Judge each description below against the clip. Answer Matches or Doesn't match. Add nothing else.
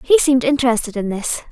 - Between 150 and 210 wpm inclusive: Matches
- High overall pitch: Matches